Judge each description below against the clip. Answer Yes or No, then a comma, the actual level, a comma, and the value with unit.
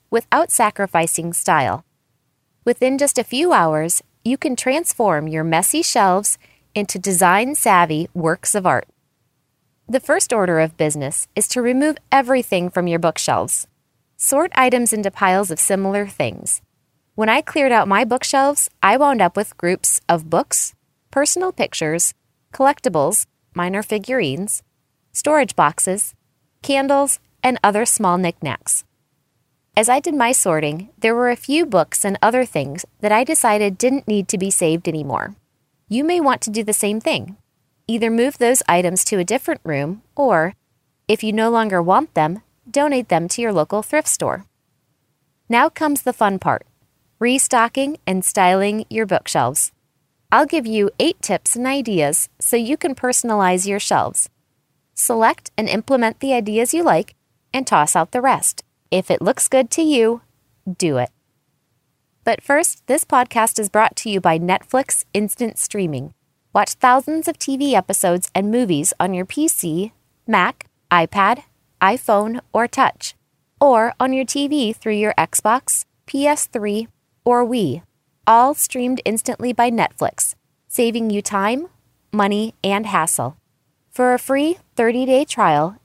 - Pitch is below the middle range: No, high, 215 Hz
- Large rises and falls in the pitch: Yes, wide, 6.8 semitones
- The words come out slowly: No, average, 150 wpm